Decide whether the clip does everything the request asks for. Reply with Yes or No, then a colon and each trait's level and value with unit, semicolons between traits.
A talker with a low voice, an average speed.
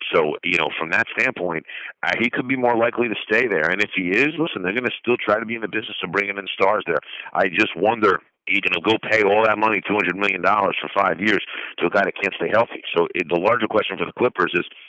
No: low, 105 Hz; fast, 270 wpm